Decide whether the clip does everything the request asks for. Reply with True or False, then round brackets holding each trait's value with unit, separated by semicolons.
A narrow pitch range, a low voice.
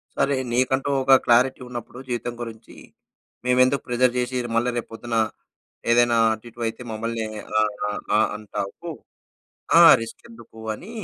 True (2.2 semitones; 120 Hz)